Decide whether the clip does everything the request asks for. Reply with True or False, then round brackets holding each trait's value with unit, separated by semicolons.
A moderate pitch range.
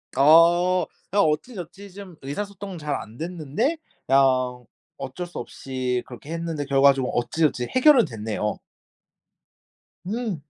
False (5.9 semitones)